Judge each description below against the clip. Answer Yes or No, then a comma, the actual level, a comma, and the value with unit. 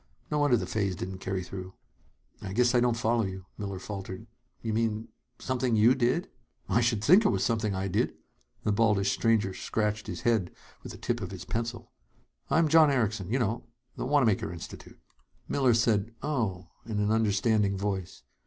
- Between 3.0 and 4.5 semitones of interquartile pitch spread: Yes, average, 3.5 semitones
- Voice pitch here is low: Yes, low, 110 Hz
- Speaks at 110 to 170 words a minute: No, average, 180 wpm